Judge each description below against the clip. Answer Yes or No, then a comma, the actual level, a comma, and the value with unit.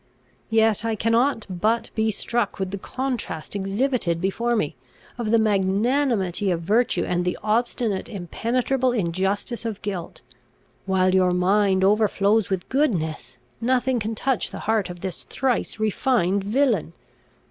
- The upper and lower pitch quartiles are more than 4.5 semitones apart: No, average, 3.9 semitones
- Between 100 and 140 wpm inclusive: Yes, slow, 135 wpm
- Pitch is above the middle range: Yes, high, 210 Hz